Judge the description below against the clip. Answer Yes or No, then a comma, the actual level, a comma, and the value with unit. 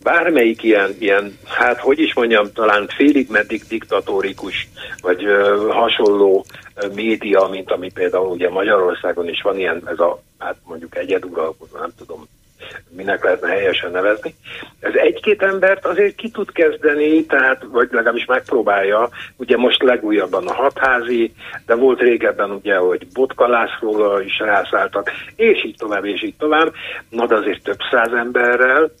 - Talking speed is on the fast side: No, average, 140 wpm